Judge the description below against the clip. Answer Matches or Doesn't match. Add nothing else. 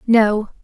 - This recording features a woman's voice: Matches